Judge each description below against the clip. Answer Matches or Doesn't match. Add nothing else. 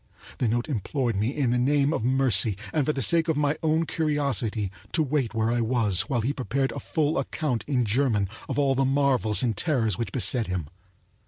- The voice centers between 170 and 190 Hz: Doesn't match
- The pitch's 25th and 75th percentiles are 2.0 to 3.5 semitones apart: Doesn't match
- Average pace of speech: Doesn't match